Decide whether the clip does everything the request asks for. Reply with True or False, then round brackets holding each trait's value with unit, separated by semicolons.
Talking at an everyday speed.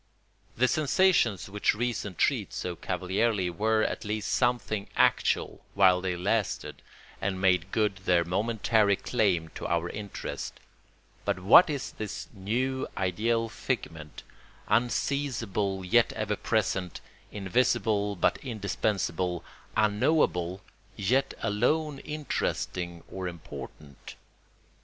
False (105 wpm)